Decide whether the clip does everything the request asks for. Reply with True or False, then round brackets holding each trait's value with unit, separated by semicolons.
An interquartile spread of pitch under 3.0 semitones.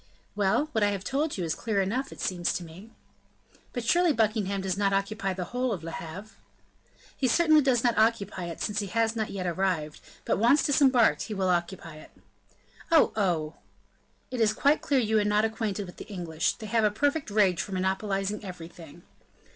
False (3.8 semitones)